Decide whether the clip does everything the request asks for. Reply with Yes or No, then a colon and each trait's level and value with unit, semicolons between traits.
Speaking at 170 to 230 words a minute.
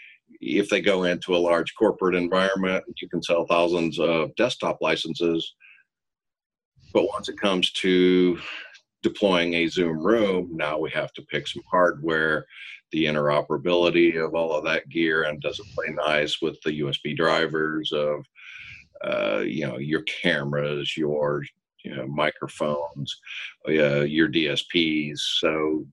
No: average, 140 wpm